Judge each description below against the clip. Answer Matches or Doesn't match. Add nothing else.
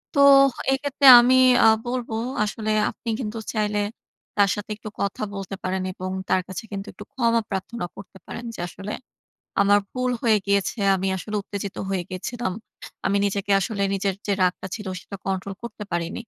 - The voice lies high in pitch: Matches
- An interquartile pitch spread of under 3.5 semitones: Matches